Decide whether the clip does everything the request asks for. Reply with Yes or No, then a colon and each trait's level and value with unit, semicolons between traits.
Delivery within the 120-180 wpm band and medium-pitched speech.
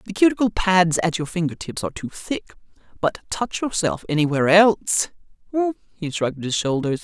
Yes: average, 160 wpm; medium, 180 Hz